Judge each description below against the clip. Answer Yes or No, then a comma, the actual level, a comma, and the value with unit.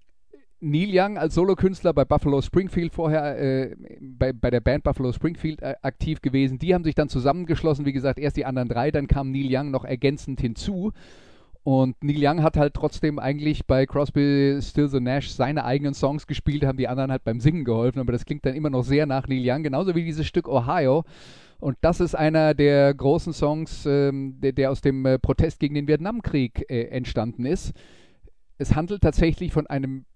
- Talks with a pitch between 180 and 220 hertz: No, medium, 140 Hz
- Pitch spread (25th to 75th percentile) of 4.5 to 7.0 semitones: No, average, 2.7 semitones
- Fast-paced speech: Yes, fast, 195 wpm